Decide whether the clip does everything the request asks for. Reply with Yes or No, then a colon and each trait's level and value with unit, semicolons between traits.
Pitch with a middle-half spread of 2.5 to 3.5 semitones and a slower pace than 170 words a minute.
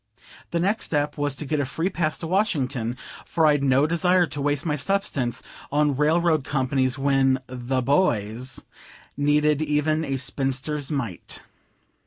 Yes: average, 2.8 semitones; average, 150 wpm